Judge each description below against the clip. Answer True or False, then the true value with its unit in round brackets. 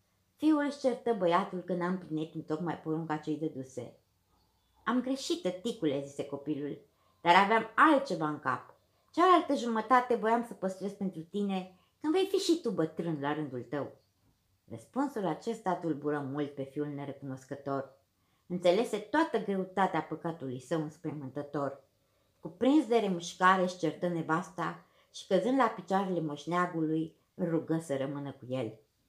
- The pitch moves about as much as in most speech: False (6.0 semitones)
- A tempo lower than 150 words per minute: True (140 wpm)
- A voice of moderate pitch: True (165 Hz)